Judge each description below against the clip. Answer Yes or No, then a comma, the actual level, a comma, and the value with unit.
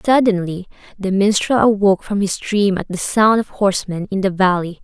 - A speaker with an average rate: Yes, average, 185 wpm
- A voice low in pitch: No, high, 195 Hz